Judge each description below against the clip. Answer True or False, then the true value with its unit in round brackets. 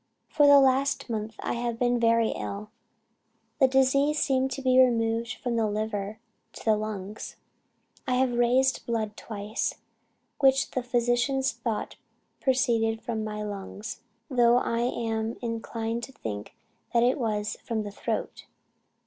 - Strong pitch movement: False (2.8 semitones)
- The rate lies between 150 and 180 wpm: False (140 wpm)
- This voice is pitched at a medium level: False (235 Hz)